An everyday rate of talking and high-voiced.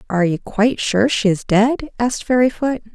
Yes: average, 185 wpm; high, 220 Hz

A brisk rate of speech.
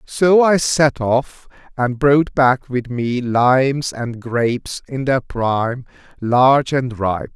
No: average, 145 wpm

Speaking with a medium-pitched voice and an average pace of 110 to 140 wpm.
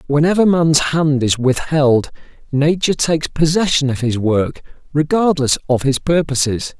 Yes: medium, 145 Hz; slow, 135 wpm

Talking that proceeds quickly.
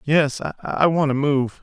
No: average, 185 wpm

